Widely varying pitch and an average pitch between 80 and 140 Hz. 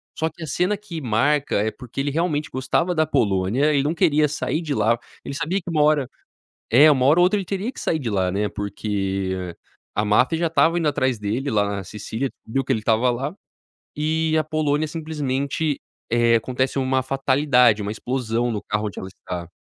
Yes: wide, 5.9 semitones; low, 135 Hz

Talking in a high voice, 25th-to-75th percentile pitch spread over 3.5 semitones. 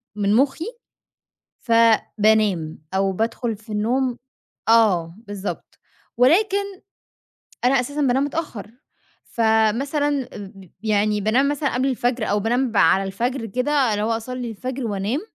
Yes: high, 230 Hz; average, 4.1 semitones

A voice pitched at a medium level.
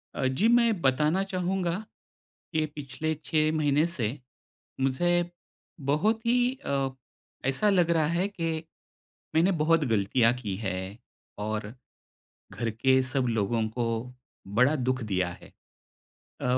Yes: medium, 145 Hz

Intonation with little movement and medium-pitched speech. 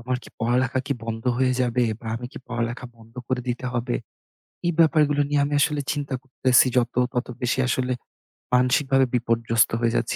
No: narrow, 2.1 semitones; low, 125 Hz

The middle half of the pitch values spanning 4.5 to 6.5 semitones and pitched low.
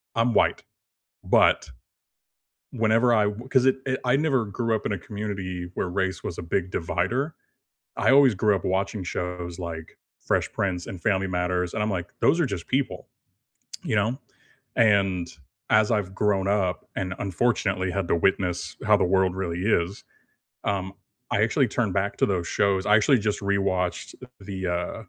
No: average, 3.0 semitones; low, 100 Hz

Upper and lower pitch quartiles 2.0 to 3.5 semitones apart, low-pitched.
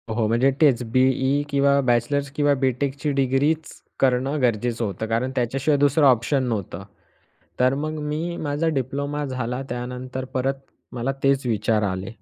Yes: average, 2.7 semitones; low, 130 Hz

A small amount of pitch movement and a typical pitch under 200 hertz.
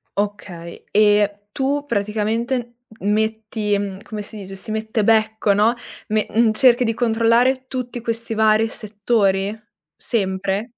No: narrow, 2.2 semitones; high, 220 Hz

